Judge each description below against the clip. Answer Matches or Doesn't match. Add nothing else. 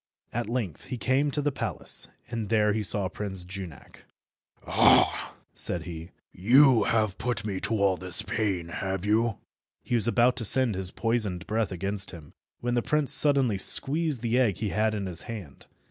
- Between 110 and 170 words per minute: Doesn't match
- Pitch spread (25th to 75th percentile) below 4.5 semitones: Matches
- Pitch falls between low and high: Doesn't match